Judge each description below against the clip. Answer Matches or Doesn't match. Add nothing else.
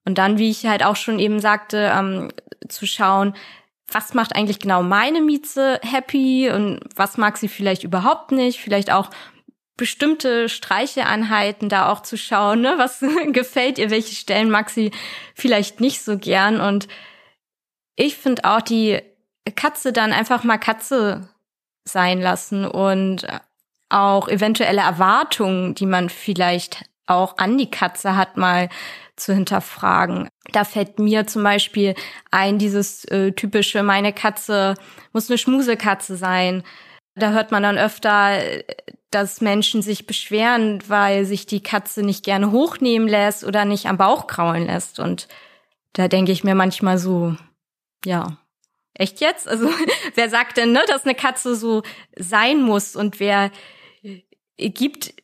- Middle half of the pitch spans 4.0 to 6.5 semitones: Doesn't match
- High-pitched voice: Matches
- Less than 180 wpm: Matches